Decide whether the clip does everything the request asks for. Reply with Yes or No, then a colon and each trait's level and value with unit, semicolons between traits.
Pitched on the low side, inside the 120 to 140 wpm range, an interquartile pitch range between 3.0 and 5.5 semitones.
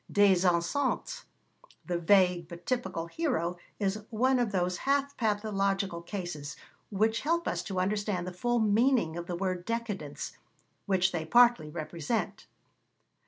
No: high, 195 Hz; slow, 135 wpm; average, 4.6 semitones